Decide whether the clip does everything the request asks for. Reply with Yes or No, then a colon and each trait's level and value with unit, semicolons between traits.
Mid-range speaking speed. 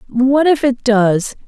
Yes: average, 165 wpm